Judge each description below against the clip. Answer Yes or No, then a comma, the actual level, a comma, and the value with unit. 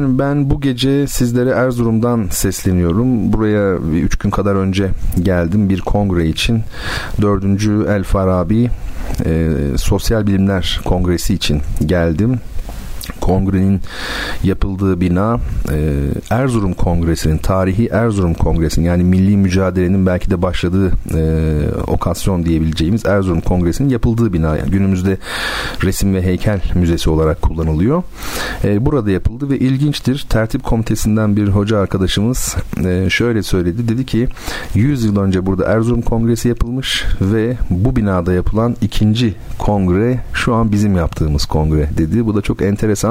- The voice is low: Yes, very low, 95 Hz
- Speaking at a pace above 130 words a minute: No, average, 125 wpm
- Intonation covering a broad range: No, average, 4.1 semitones